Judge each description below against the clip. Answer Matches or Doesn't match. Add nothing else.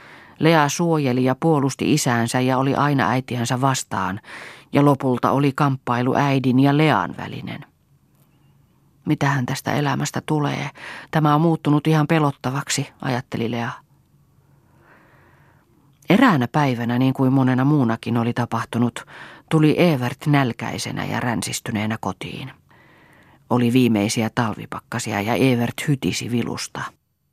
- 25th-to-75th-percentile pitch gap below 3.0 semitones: Doesn't match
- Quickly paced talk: Doesn't match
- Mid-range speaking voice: Doesn't match